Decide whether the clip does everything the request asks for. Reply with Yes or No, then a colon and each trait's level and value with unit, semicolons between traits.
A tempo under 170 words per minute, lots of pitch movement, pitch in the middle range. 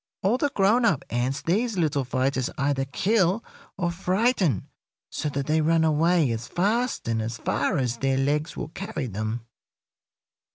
Yes: average, 160 wpm; wide, 6.5 semitones; medium, 155 Hz